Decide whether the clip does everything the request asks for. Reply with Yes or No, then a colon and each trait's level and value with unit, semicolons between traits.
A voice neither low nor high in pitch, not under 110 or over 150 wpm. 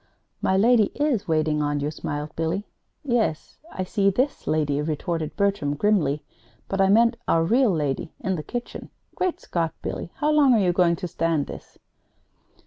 No: medium, 180 Hz; average, 175 wpm